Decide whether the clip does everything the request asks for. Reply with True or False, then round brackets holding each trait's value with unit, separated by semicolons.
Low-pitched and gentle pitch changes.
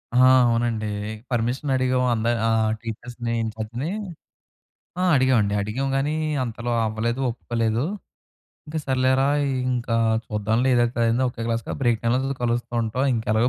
True (120 Hz; 2.3 semitones)